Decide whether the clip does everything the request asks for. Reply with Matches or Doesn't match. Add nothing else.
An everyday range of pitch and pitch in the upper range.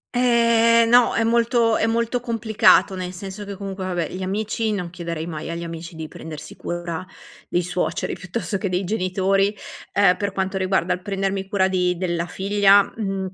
Matches